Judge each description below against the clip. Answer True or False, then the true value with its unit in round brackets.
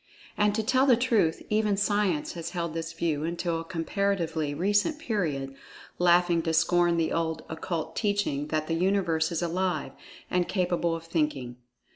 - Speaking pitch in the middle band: True (170 Hz)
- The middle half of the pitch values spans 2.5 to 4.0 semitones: True (3.6 semitones)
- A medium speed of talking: True (160 wpm)